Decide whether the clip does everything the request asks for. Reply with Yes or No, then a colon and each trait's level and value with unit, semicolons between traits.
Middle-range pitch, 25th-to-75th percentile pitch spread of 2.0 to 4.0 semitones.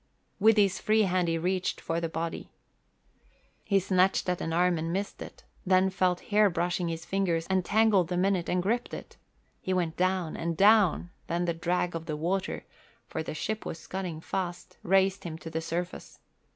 Yes: medium, 180 Hz; narrow, 2.4 semitones